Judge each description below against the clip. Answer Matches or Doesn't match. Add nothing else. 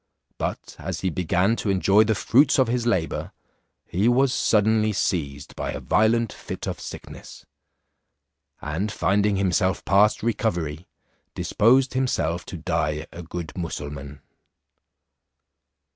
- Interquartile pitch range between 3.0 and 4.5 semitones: Doesn't match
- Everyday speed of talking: Doesn't match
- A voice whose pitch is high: Doesn't match